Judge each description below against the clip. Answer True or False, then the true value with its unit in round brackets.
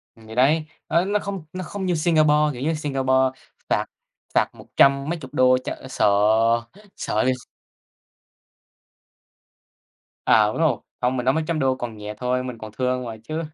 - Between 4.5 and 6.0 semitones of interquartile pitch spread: False (3.9 semitones)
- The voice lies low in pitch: True (130 Hz)